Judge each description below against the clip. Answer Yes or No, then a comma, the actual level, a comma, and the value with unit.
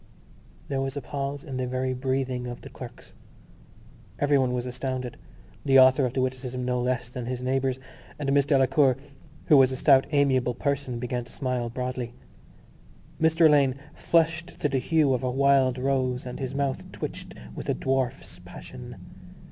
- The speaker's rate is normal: Yes, average, 170 wpm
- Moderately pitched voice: No, low, 130 Hz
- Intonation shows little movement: Yes, narrow, 1.7 semitones